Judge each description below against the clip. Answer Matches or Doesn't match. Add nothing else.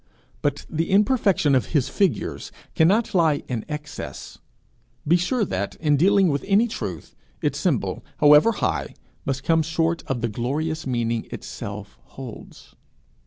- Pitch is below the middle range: Doesn't match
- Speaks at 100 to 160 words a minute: Matches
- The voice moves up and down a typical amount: Doesn't match